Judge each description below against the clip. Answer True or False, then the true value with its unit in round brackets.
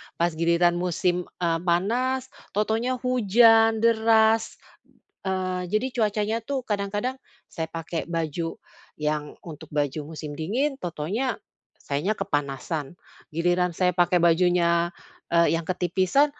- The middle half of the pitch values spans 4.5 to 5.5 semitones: True (4.9 semitones)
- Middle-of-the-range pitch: True (180 Hz)